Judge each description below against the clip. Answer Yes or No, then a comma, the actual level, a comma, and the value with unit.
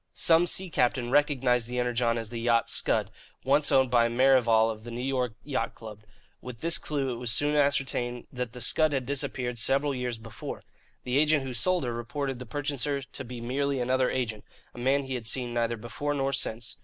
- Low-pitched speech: Yes, low, 125 Hz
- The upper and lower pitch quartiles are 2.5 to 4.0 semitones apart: Yes, average, 2.8 semitones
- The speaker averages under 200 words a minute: No, fast, 205 wpm